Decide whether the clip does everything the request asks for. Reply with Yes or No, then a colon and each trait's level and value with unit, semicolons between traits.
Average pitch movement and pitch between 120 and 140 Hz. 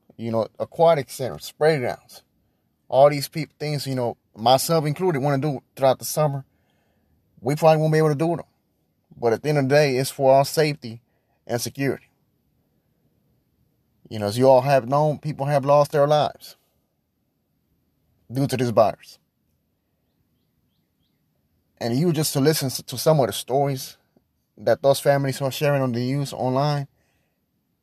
Yes: average, 3.8 semitones; low, 135 Hz